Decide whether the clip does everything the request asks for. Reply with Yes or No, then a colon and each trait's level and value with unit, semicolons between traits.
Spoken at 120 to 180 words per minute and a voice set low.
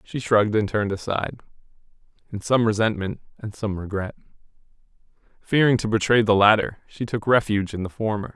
Yes: average, 160 wpm; low, 105 Hz